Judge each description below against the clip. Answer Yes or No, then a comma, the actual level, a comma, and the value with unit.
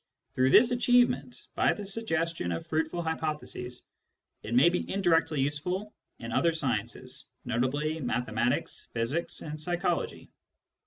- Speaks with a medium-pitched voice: Yes, medium, 155 Hz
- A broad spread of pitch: Yes, wide, 5.8 semitones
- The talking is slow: Yes, slow, 120 wpm